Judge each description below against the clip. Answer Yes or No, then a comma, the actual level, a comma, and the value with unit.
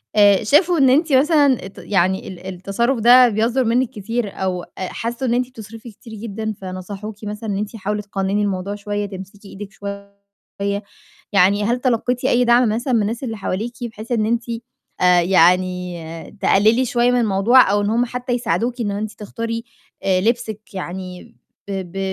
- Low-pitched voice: No, high, 215 Hz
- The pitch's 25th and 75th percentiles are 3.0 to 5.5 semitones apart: Yes, average, 3.5 semitones